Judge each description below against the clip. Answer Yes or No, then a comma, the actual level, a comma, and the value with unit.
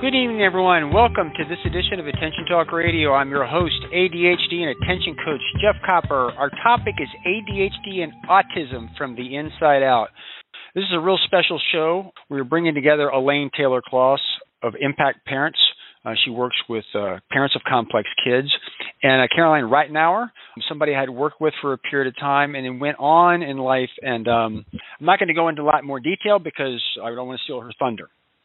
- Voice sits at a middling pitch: Yes, medium, 150 Hz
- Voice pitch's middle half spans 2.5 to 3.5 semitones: No, average, 4.3 semitones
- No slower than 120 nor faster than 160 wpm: No, average, 200 wpm